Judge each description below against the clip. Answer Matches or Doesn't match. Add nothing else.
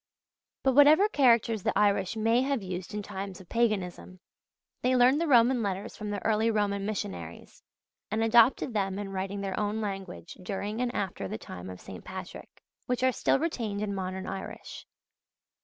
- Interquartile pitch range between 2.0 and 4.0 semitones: Matches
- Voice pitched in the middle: Doesn't match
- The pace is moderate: Matches